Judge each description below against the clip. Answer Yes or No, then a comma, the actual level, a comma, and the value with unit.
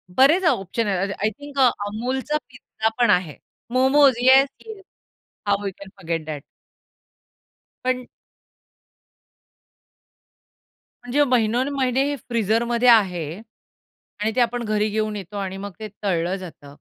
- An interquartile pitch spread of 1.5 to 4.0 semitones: No, average, 4.7 semitones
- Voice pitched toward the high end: Yes, high, 225 Hz